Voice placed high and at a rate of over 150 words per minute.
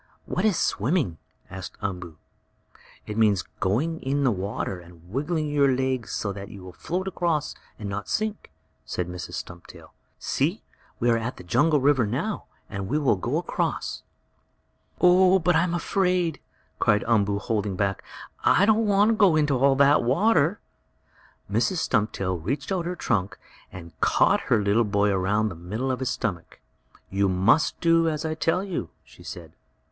No: low, 125 Hz; average, 165 wpm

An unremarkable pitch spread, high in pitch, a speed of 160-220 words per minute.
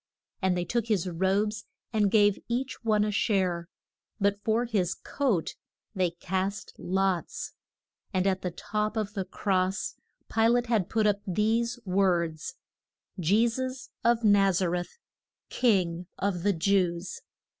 No: average, 3.1 semitones; high, 200 Hz; average, 145 wpm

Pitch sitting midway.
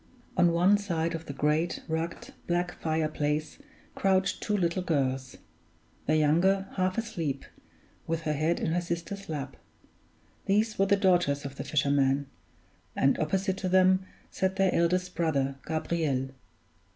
Yes: medium, 170 Hz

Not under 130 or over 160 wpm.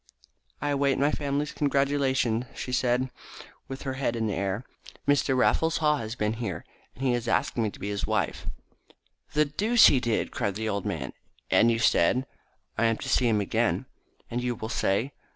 No: average, 195 wpm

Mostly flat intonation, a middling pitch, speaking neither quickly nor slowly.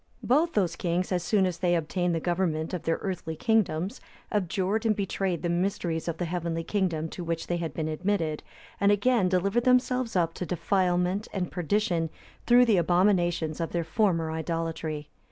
No: average, 3.3 semitones; medium, 180 Hz; average, 175 wpm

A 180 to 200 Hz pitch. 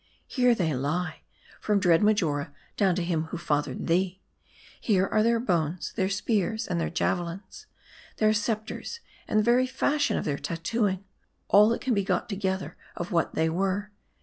Yes: high, 190 Hz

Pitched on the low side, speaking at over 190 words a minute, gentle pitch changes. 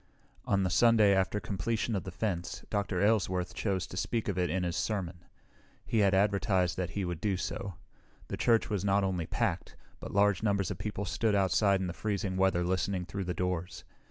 Yes: very low, 95 Hz; average, 200 wpm; narrow, 2.2 semitones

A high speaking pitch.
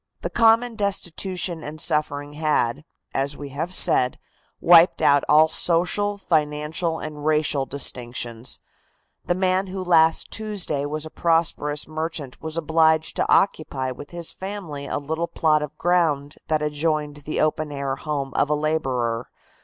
No: medium, 155 Hz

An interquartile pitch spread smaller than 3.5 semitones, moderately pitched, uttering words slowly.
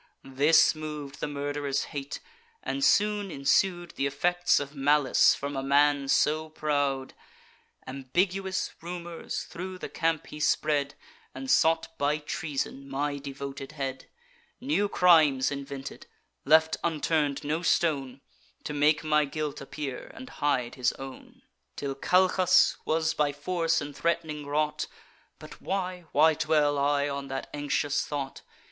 Yes: average, 2.7 semitones; medium, 150 Hz; slow, 130 wpm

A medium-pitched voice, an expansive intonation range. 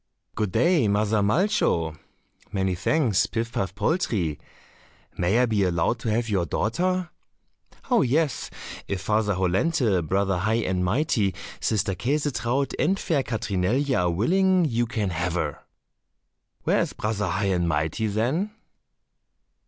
No: low, 110 Hz; wide, 6.2 semitones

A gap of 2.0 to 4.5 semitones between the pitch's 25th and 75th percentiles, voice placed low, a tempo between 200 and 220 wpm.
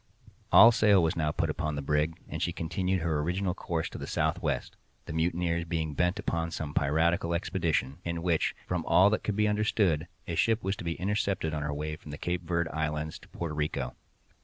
Yes: average, 2.7 semitones; very low, 85 Hz; fast, 205 wpm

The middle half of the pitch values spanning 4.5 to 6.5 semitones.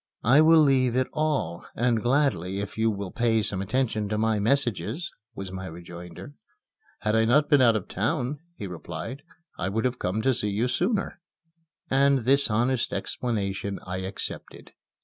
Yes: average, 5.2 semitones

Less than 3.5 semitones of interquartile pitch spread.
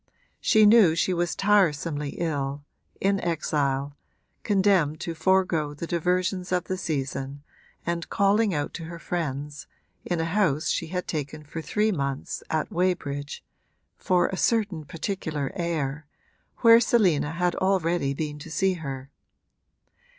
No: average, 4.1 semitones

